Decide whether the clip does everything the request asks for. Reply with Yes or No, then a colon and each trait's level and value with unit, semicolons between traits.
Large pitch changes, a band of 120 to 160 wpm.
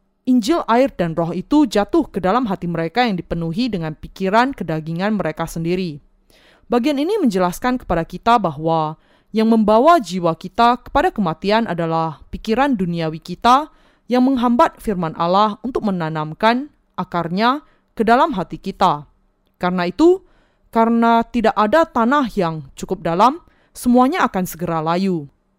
Yes: wide, 6.5 semitones; average, 135 wpm